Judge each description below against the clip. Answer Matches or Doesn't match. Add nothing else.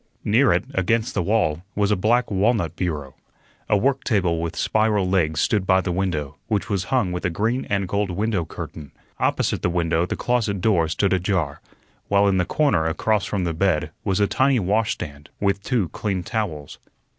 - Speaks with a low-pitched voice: Matches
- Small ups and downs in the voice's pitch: Doesn't match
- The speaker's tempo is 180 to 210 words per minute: Matches